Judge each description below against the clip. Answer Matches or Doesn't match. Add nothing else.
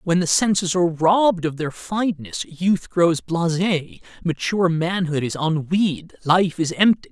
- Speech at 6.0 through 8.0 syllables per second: Doesn't match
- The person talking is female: Doesn't match